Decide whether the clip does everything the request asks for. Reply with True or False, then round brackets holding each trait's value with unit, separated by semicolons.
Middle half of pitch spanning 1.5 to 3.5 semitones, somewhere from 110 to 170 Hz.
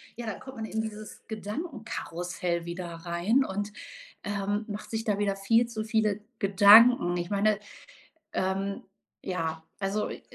False (2.7 semitones; 205 Hz)